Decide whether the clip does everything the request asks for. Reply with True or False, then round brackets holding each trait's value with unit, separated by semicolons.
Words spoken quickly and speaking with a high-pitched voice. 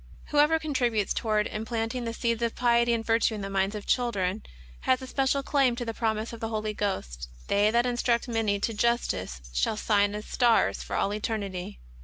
True (210 wpm; 225 Hz)